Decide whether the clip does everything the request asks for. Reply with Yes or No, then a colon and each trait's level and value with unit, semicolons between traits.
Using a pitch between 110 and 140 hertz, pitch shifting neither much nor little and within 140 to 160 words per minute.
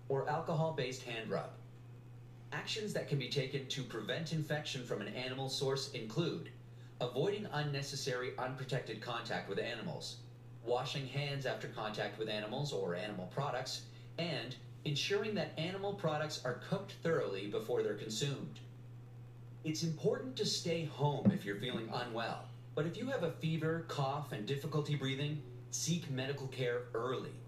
Yes: low, 135 Hz; average, 4.1 semitones; average, 145 wpm